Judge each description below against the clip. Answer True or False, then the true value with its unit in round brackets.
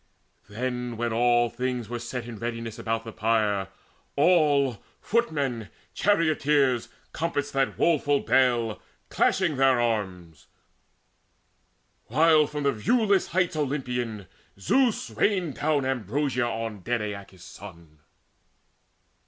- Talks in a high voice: False (125 Hz)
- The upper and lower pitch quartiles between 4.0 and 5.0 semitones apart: True (4.5 semitones)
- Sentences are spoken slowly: True (110 wpm)